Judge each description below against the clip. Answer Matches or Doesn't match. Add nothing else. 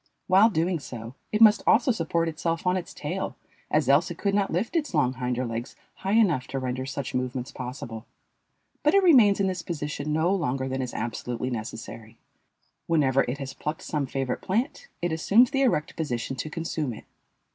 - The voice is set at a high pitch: Doesn't match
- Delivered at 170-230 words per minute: Matches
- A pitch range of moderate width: Doesn't match